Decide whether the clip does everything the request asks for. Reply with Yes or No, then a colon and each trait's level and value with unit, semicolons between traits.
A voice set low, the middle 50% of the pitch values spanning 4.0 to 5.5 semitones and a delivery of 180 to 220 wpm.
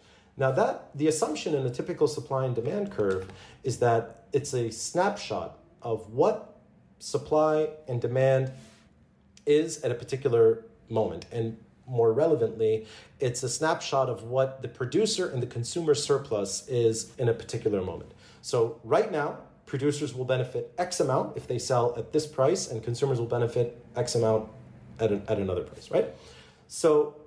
No: low, 130 Hz; average, 4.6 semitones; average, 160 wpm